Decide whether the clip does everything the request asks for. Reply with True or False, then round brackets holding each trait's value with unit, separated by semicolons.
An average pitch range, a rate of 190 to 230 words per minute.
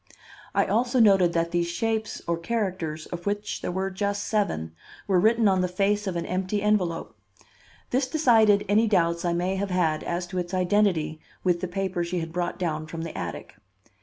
True (3.2 semitones; 195 wpm)